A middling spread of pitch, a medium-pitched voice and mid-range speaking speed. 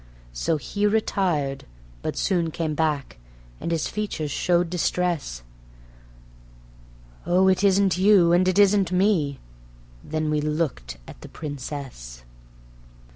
No: average, 4.2 semitones; medium, 170 Hz; slow, 125 wpm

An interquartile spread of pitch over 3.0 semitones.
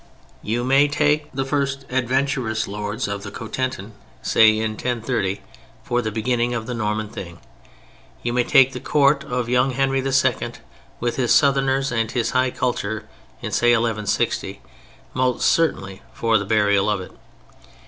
Yes: average, 3.5 semitones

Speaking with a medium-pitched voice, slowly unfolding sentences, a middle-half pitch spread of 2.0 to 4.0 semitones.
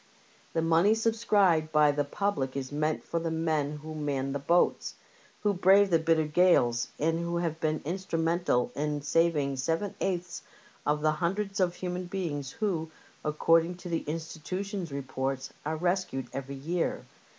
No: medium, 165 Hz; average, 160 wpm; average, 3.3 semitones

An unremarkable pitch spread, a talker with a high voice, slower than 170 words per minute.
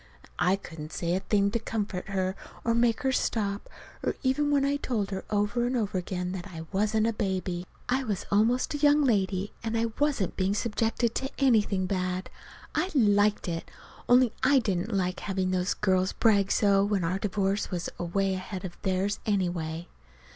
No: average, 3.5 semitones; high, 200 Hz; average, 185 wpm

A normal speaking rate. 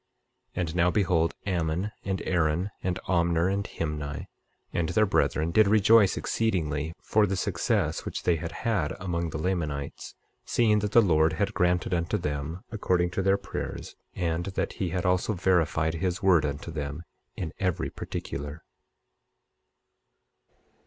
Yes: average, 150 wpm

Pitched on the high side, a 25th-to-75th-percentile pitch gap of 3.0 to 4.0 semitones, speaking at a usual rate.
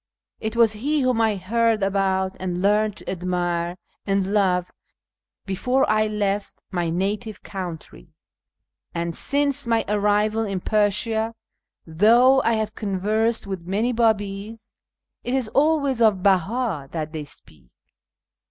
No: high, 205 Hz; average, 3.4 semitones; slow, 130 wpm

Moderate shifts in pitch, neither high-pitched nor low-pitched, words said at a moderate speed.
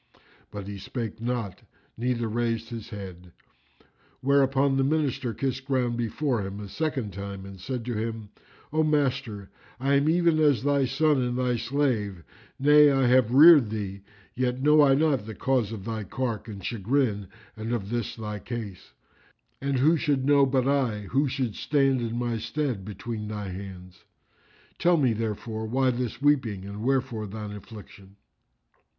No: average, 4.4 semitones; low, 120 Hz; average, 165 wpm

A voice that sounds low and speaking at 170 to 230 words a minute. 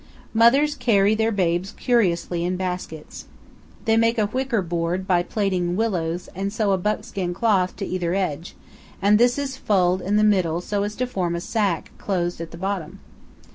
No: high, 195 Hz; average, 175 wpm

